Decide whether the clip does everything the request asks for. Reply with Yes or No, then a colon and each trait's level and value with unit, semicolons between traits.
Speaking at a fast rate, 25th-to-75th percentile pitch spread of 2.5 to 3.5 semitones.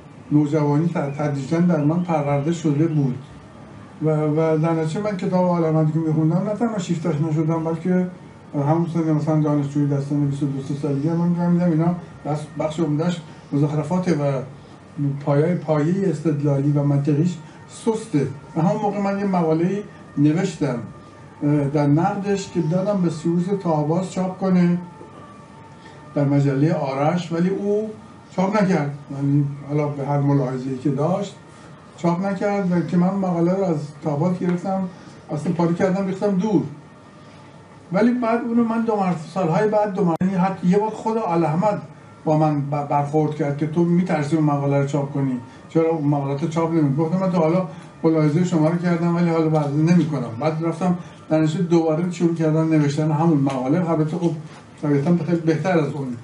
Yes: fast, 165 wpm; average, 3.0 semitones